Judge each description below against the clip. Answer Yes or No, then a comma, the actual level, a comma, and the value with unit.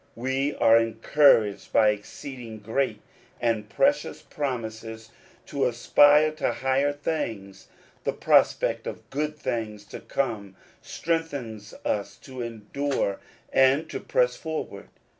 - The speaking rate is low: Yes, slow, 115 wpm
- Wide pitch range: No, average, 4.7 semitones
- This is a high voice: No, low, 125 Hz